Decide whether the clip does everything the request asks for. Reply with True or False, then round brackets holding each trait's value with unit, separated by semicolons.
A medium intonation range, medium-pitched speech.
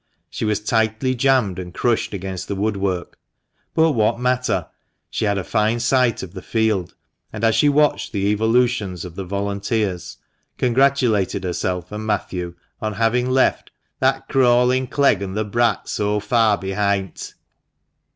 False (3.9 semitones; 110 Hz)